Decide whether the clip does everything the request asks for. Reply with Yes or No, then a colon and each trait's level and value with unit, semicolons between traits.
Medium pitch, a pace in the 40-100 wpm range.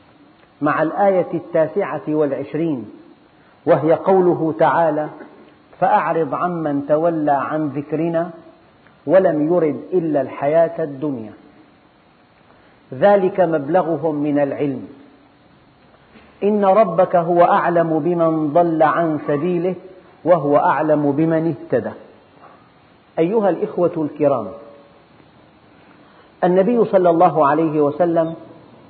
Yes: medium, 165 Hz; average, 85 wpm